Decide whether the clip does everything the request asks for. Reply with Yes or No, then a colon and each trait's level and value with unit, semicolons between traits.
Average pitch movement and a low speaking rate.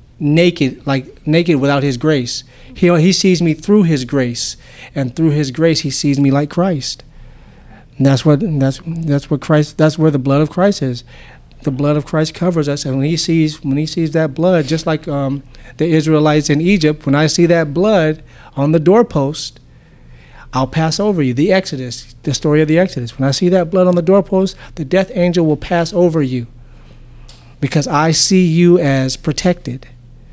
No: average, 3.7 semitones; average, 195 wpm